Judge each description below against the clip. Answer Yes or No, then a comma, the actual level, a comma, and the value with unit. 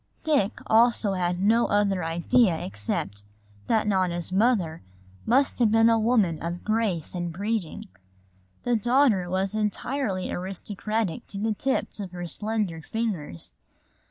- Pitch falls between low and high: No, high, 200 Hz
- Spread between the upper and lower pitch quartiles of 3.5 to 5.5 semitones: Yes, average, 4.3 semitones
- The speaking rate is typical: No, slow, 130 wpm